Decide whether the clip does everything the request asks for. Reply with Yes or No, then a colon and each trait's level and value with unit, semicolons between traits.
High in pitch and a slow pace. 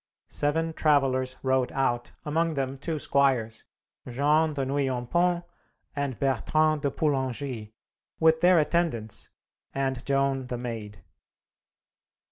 No: low, 135 Hz; slow, 105 wpm